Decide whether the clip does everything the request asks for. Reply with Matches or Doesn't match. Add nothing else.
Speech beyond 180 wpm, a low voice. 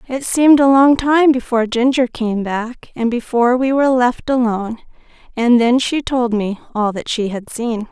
Doesn't match